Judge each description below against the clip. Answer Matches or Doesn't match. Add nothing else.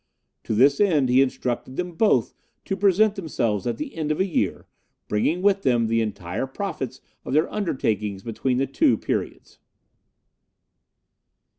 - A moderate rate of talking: Matches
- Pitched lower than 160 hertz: Matches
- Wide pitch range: Matches